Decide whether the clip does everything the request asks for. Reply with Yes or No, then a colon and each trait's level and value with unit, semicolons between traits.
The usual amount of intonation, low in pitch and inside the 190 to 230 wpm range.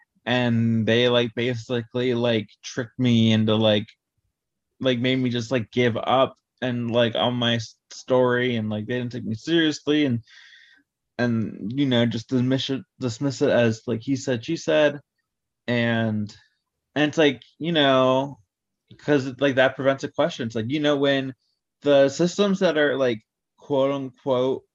No: average, 3.1 semitones; low, 125 Hz; average, 160 wpm